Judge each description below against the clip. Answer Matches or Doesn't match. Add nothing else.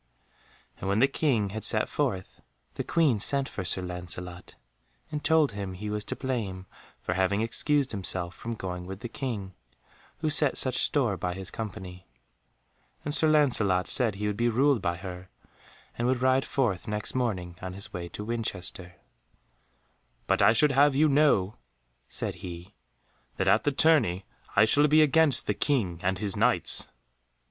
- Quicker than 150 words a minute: Matches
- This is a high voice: Doesn't match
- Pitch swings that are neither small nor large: Doesn't match